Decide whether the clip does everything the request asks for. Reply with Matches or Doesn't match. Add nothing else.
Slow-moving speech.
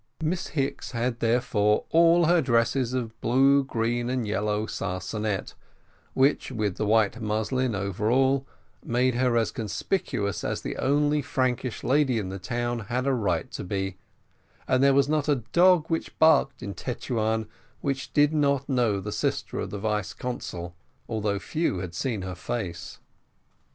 Doesn't match